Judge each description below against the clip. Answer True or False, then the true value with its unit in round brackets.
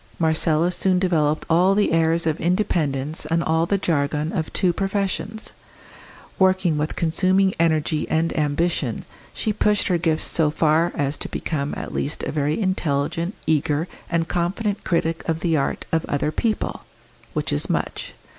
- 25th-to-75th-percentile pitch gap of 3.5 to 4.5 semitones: False (3.1 semitones)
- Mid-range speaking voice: True (165 Hz)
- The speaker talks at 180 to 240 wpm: False (155 wpm)